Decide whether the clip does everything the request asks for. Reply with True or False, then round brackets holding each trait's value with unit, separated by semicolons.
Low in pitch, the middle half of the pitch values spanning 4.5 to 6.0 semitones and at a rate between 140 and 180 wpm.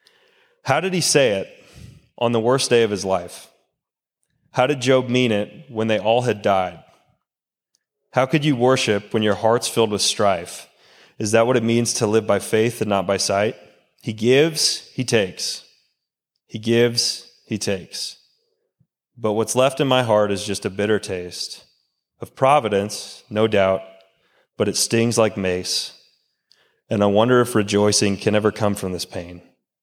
False (110 Hz; 3.6 semitones; 170 wpm)